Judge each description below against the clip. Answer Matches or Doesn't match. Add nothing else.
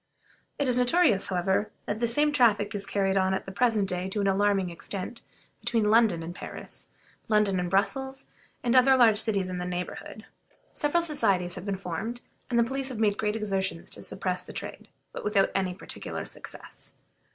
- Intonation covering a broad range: Doesn't match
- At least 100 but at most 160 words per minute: Doesn't match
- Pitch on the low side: Doesn't match